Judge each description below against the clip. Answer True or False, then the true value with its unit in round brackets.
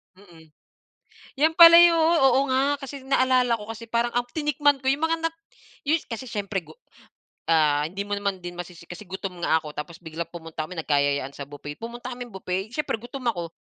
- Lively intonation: True (7.9 semitones)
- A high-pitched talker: True (210 Hz)